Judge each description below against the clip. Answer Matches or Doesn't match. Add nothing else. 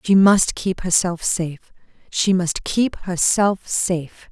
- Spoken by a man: Doesn't match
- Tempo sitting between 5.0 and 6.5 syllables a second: Doesn't match